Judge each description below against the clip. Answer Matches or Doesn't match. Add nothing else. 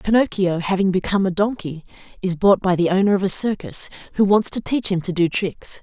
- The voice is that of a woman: Matches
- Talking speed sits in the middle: Doesn't match